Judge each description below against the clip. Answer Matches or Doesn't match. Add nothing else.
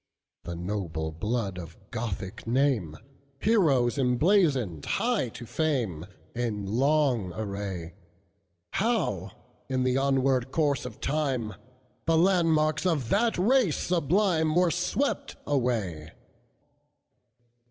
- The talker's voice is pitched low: Matches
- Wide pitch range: Matches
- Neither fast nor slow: Doesn't match